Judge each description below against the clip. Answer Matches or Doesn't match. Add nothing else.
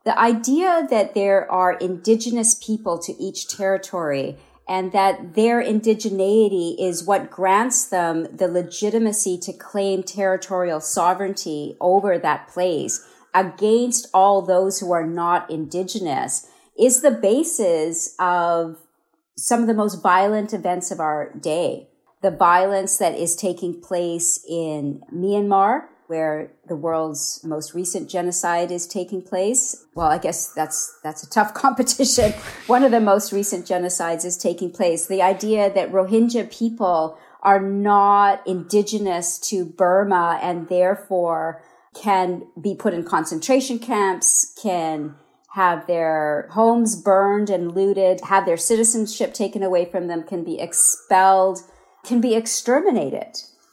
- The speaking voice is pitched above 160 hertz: Matches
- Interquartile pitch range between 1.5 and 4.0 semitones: Matches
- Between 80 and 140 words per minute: Matches